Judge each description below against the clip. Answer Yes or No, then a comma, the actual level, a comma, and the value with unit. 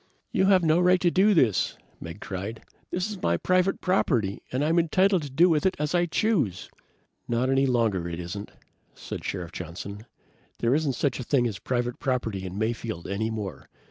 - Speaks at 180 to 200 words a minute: Yes, average, 185 wpm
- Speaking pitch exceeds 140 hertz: No, low, 125 Hz